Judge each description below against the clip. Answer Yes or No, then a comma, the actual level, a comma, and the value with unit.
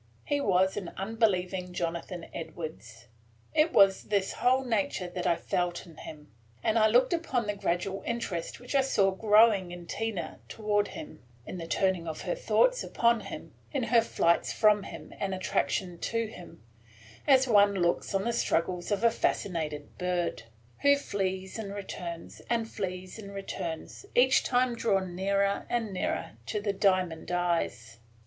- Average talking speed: Yes, average, 160 wpm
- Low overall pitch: No, high, 195 Hz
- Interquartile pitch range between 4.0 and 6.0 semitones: Yes, average, 4.3 semitones